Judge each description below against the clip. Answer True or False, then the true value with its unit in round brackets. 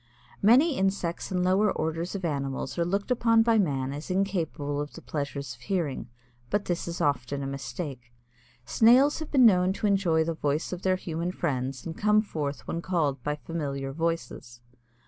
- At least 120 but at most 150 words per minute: False (180 wpm)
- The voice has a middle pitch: True (170 Hz)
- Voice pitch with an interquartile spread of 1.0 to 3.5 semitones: False (5.5 semitones)